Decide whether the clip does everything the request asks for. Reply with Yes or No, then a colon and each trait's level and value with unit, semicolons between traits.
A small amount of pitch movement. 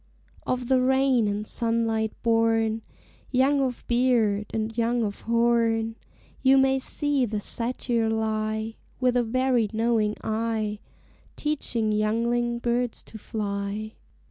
Yes: narrow, 2.2 semitones